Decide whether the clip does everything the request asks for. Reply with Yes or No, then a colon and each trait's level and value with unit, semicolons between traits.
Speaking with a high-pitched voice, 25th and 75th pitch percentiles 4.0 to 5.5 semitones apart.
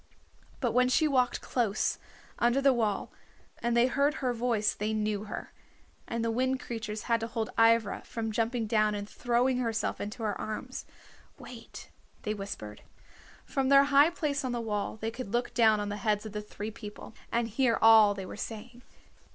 No: high, 230 Hz; average, 2.7 semitones